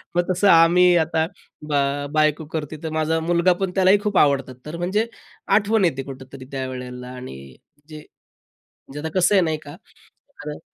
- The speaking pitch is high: No, medium, 160 Hz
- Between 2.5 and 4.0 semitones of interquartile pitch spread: No, average, 4.4 semitones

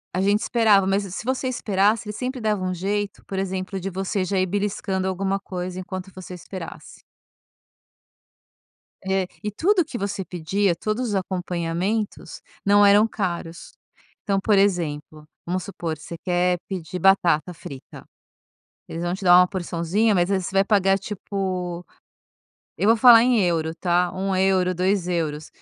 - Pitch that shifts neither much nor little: No, narrow, 2.3 semitones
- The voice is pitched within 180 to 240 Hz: Yes, high, 190 Hz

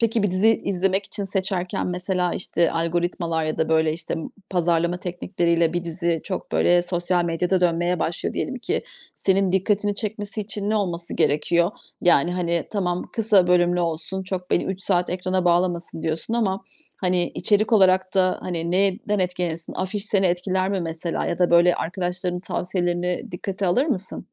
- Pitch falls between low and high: Yes, medium, 180 Hz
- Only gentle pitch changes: Yes, narrow, 2.0 semitones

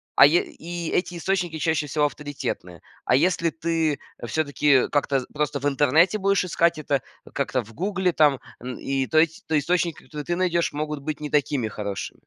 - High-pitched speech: No, medium, 150 Hz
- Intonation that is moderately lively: Yes, average, 3.3 semitones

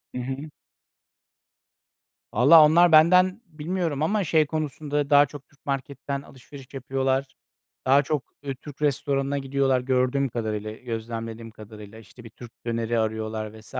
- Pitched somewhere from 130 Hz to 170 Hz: Yes, low, 135 Hz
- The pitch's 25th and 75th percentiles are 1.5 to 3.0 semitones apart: No, average, 4.1 semitones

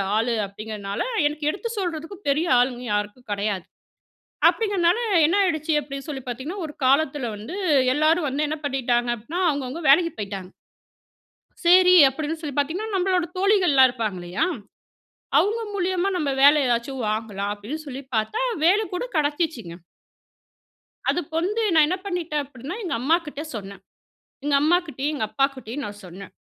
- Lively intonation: Yes, wide, 6.3 semitones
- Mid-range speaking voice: No, very high, 290 Hz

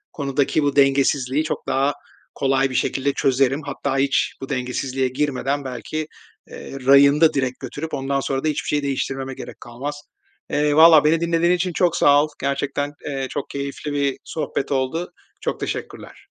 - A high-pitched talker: No, medium, 140 Hz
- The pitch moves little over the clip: Yes, narrow, 1.6 semitones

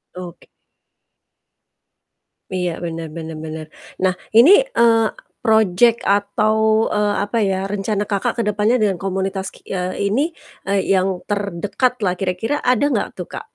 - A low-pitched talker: No, high, 200 Hz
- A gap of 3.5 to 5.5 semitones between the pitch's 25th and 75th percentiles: No, average, 3.0 semitones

